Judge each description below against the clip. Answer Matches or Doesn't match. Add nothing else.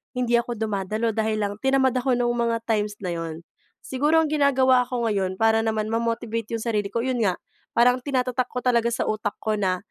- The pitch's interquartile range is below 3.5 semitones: Matches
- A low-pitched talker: Doesn't match